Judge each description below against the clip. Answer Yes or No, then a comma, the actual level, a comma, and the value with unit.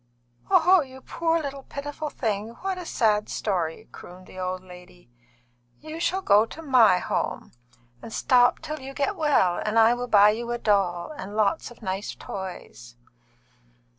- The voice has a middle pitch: No, high, 225 Hz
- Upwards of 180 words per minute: No, average, 165 wpm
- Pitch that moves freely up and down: Yes, wide, 7.4 semitones